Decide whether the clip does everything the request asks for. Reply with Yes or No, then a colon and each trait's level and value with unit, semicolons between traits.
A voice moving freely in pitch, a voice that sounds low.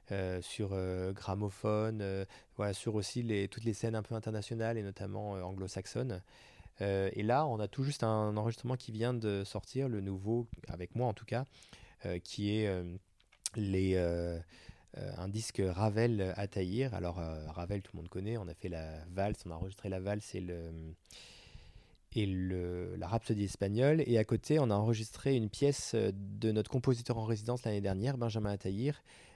No: average, 3.5 semitones; low, 105 Hz